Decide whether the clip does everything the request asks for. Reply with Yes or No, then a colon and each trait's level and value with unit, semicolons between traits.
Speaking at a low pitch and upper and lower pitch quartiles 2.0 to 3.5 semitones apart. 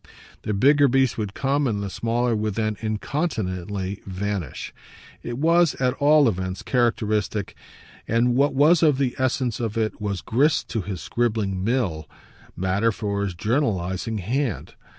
No: low, 110 Hz; average, 4.6 semitones